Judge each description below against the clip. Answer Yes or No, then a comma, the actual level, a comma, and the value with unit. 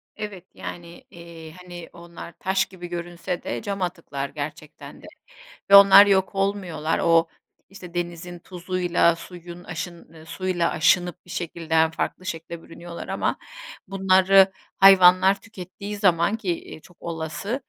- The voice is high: No, medium, 175 Hz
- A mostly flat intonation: Yes, narrow, 2.1 semitones